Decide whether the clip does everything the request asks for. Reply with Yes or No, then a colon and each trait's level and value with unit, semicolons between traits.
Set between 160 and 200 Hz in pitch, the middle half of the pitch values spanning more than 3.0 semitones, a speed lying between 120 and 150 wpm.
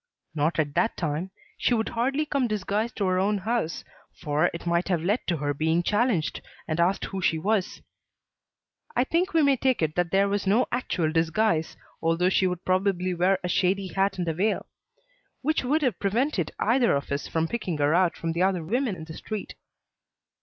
No: medium, 185 Hz; average, 5.0 semitones; average, 200 wpm